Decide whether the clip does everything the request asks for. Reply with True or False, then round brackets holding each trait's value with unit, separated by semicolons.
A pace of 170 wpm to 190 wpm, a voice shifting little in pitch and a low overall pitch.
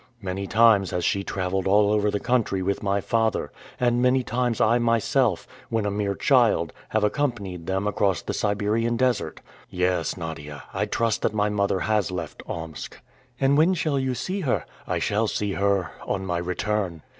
False (180 wpm; 3.6 semitones; 105 Hz)